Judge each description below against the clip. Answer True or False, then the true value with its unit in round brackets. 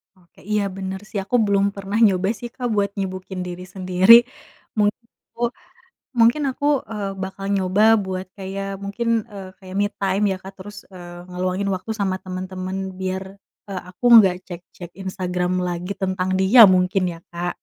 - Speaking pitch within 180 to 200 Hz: True (190 Hz)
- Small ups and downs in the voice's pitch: True (1.5 semitones)